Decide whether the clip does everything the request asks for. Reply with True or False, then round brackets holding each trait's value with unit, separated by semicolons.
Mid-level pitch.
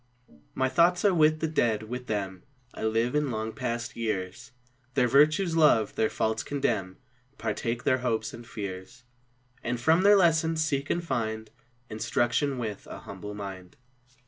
False (120 Hz)